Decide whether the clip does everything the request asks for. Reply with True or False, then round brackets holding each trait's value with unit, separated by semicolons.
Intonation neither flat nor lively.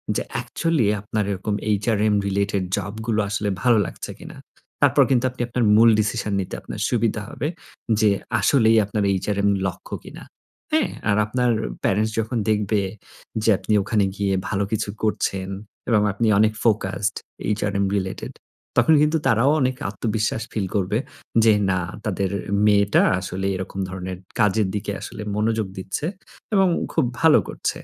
False (2.2 semitones)